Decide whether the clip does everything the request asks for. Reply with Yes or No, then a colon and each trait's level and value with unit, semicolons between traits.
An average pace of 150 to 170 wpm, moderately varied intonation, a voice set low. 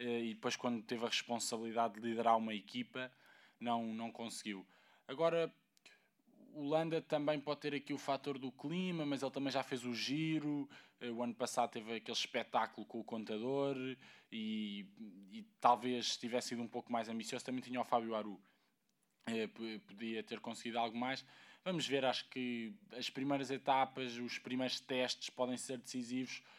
Yes: average, 160 wpm; average, 3.5 semitones; low, 125 Hz